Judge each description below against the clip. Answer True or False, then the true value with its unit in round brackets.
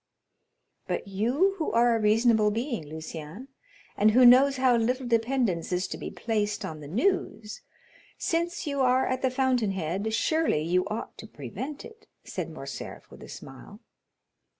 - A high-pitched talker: True (230 Hz)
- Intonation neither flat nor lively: True (4.7 semitones)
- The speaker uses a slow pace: False (160 wpm)